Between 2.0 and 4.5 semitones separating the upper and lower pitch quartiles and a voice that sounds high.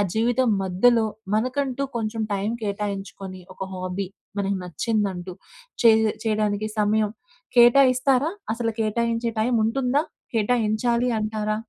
Yes: average, 2.9 semitones; high, 220 Hz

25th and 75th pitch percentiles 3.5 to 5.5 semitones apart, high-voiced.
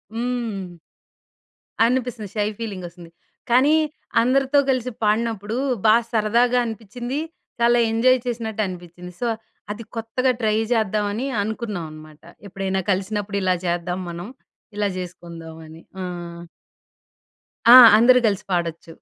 Yes: average, 4.7 semitones; high, 210 Hz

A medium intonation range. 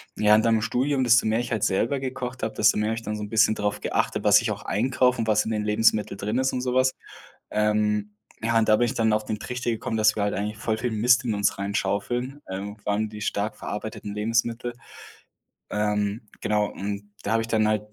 No: narrow, 2.0 semitones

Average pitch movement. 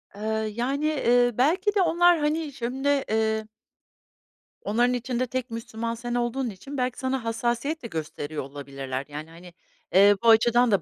Yes: average, 3.7 semitones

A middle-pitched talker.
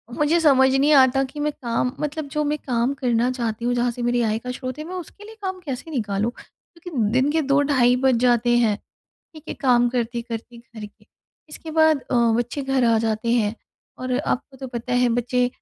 No: very high, 250 Hz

